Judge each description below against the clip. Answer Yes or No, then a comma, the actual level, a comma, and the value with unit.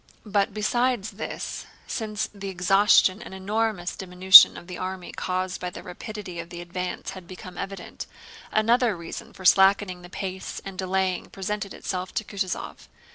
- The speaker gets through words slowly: No, average, 155 wpm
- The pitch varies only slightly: Yes, narrow, 2.2 semitones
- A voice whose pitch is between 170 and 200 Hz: Yes, high, 190 Hz